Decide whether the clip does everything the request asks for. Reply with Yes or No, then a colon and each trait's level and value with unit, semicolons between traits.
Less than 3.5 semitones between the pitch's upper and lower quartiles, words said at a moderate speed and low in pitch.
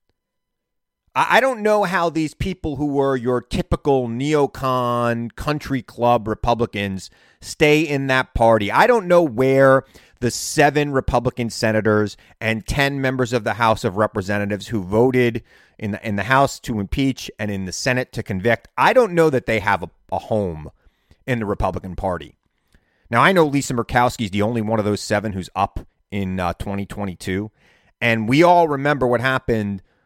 No: average, 4.6 semitones; average, 170 wpm; low, 120 Hz